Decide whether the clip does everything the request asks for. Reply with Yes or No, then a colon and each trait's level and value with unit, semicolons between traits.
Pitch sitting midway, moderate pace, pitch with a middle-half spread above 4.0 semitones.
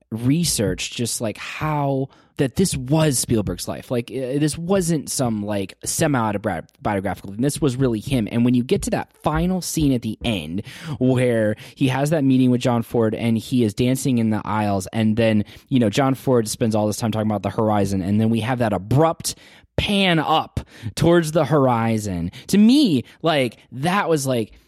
No: low, 125 Hz; average, 185 wpm; average, 5.2 semitones